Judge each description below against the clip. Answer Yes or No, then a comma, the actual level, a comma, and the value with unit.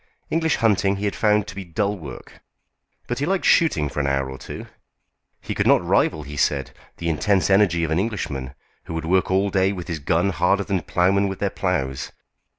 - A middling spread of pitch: Yes, average, 4.3 semitones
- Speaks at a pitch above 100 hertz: No, very low, 95 Hz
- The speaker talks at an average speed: No, fast, 210 wpm